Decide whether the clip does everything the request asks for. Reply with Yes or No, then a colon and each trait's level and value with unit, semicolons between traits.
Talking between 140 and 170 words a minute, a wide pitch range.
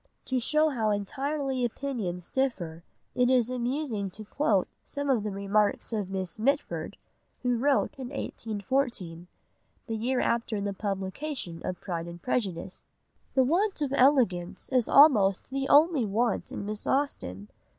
Yes: average, 145 wpm; wide, 5.7 semitones